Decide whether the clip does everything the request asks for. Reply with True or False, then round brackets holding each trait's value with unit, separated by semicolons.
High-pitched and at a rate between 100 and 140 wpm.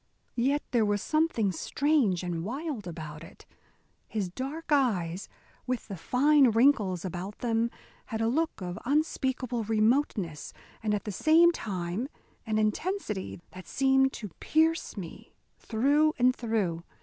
True (225 Hz; 135 wpm)